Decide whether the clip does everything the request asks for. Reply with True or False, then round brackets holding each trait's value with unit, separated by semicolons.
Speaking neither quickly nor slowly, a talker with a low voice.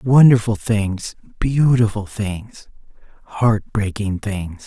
False (90 wpm; 110 Hz)